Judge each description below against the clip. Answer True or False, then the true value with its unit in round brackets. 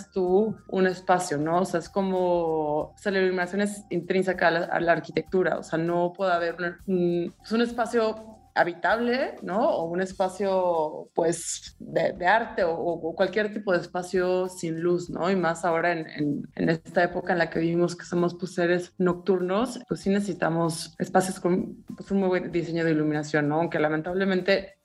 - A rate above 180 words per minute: True (190 wpm)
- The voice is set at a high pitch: False (180 Hz)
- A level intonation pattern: True (2.3 semitones)